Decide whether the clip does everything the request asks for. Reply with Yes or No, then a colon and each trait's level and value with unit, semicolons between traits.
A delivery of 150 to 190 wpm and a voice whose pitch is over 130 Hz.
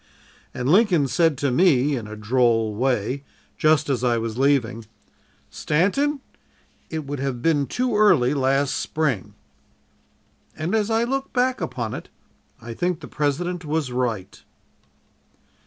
No: average, 140 wpm; medium, 140 Hz